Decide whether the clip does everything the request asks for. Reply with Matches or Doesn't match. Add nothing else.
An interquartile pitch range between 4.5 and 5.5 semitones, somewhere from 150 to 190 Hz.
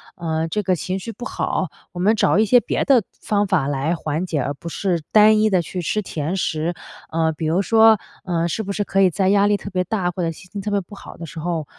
Doesn't match